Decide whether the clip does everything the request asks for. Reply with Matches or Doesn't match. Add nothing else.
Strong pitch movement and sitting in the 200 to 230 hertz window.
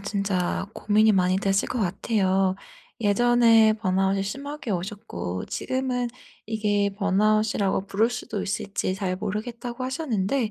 Doesn't match